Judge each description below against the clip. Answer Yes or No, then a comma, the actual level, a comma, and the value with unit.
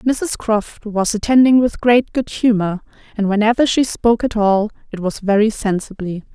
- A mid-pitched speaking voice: No, high, 220 Hz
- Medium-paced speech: Yes, average, 170 wpm